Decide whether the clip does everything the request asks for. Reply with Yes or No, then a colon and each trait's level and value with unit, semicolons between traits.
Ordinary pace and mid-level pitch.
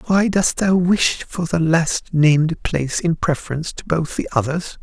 Yes: average, 185 wpm; medium, 165 Hz